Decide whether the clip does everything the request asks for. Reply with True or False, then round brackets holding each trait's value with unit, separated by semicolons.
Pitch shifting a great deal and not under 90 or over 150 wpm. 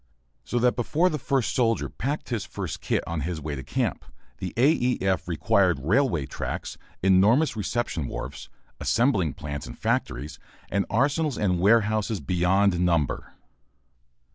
True (6.2 semitones; 145 wpm)